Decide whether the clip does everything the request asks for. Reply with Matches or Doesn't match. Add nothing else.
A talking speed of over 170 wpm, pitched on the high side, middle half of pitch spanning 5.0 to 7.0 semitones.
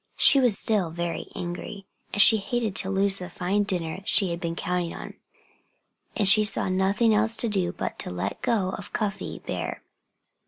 Doesn't match